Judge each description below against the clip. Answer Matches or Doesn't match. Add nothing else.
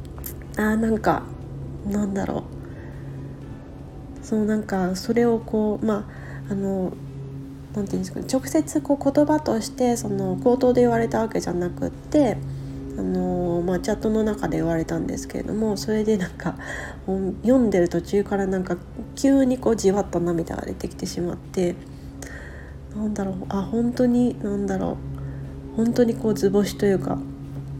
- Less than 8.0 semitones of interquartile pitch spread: Doesn't match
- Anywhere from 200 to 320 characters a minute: Matches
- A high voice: Matches